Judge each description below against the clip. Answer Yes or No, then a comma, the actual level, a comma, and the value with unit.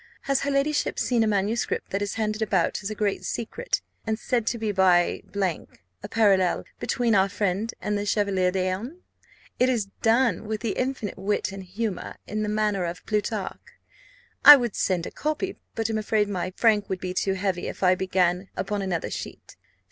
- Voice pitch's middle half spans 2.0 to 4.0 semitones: Yes, average, 3.0 semitones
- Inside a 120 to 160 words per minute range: No, average, 185 wpm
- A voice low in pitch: No, high, 205 Hz